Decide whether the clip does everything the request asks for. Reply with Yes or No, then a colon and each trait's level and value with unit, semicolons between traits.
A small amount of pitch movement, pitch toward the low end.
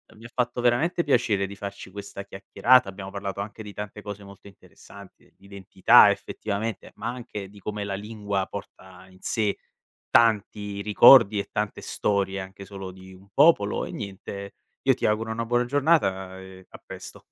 Yes: narrow, 2.3 semitones; low, 100 Hz